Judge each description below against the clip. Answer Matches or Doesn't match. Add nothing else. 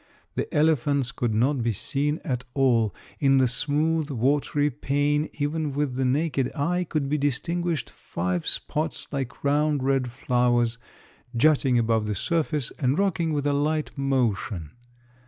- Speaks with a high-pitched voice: Doesn't match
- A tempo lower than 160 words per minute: Matches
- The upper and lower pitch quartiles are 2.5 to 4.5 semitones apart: Matches